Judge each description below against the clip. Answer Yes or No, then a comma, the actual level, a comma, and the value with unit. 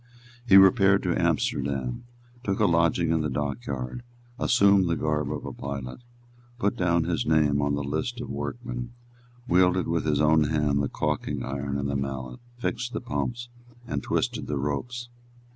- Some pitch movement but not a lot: No, wide, 5.9 semitones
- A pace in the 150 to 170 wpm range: Yes, average, 165 wpm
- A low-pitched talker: Yes, very low, 80 Hz